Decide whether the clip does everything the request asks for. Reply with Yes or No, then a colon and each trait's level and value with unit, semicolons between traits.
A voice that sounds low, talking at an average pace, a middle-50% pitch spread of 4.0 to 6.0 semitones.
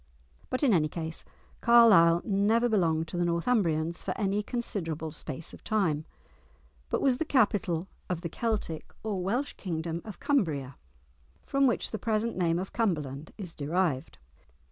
No: medium, 180 Hz; average, 150 wpm; average, 5.3 semitones